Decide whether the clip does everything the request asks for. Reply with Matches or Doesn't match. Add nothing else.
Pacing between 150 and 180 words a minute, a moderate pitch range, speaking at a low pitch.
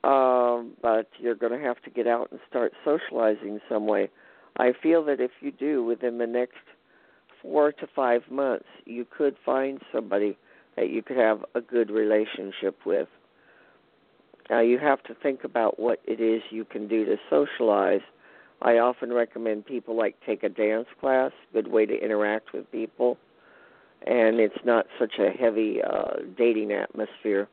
Doesn't match